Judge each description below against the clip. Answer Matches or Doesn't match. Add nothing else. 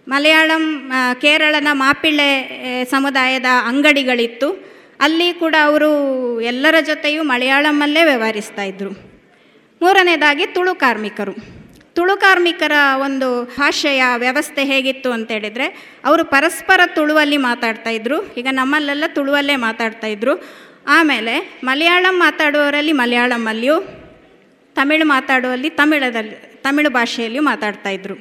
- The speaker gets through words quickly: Doesn't match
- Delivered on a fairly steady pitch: Doesn't match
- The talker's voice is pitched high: Matches